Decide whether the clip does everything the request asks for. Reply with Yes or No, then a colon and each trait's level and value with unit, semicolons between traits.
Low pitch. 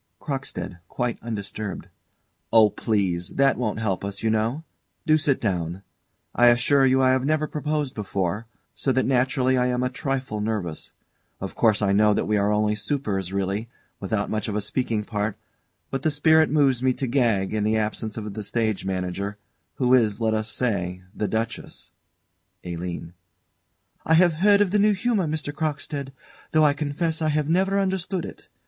Yes: low, 120 Hz